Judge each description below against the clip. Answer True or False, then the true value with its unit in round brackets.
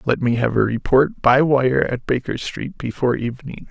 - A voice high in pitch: False (125 Hz)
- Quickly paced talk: False (195 wpm)